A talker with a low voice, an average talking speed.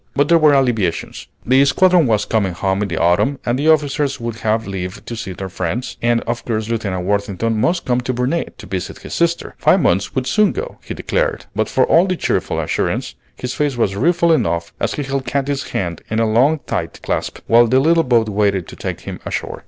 No: low, 120 Hz; fast, 220 wpm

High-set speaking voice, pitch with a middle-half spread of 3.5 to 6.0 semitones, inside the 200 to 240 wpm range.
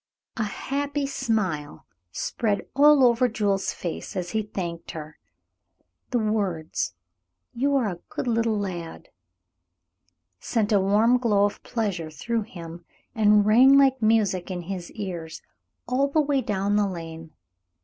No: high, 210 Hz; average, 5.1 semitones; average, 140 wpm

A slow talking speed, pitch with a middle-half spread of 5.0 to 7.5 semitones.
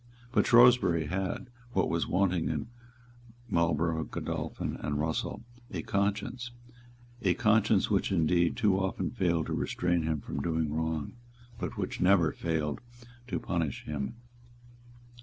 No: slow, 130 wpm; average, 3.7 semitones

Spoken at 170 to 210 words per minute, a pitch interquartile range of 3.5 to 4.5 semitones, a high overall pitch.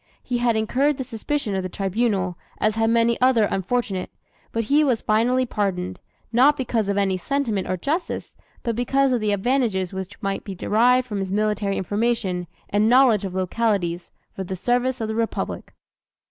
Yes: average, 175 wpm; average, 4.2 semitones; high, 220 Hz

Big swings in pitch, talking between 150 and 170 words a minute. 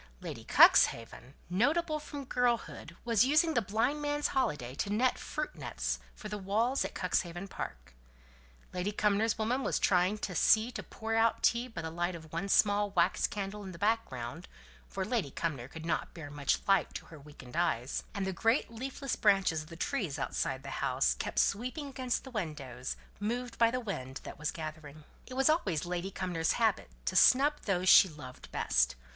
No: wide, 6.7 semitones; average, 185 wpm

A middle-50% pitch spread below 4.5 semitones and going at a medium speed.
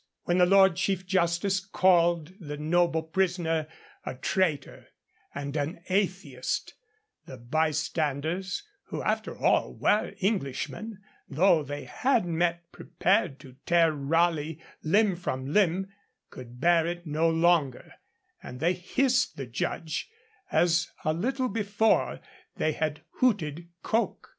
No: average, 3.8 semitones; slow, 125 wpm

